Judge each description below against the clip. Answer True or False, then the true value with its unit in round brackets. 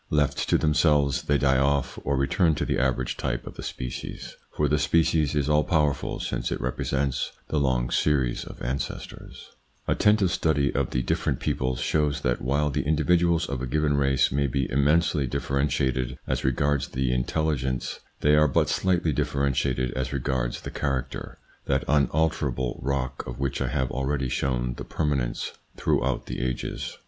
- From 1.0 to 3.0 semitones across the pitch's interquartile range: True (2.6 semitones)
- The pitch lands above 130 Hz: False (70 Hz)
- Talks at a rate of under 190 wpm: True (170 wpm)